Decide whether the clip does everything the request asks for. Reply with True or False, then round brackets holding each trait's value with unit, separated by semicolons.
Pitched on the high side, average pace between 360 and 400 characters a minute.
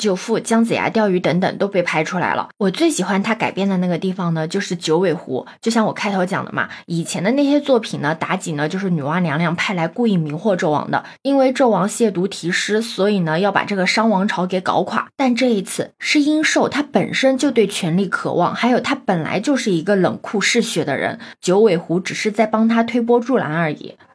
False (195 Hz; 330 characters per minute)